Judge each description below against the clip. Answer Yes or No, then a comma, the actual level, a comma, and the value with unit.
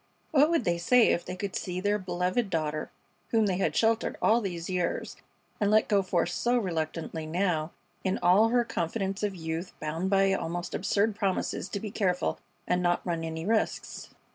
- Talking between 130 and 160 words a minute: No, average, 185 wpm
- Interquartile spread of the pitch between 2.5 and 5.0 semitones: Yes, average, 3.4 semitones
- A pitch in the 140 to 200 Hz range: Yes, medium, 185 Hz